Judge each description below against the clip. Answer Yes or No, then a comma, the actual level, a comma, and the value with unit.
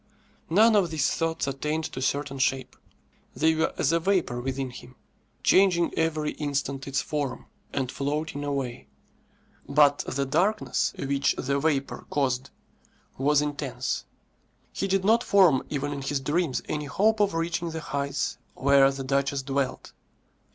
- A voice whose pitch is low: No, medium, 145 Hz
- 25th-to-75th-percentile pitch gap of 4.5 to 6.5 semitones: No, average, 3.2 semitones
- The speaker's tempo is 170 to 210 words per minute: No, average, 145 wpm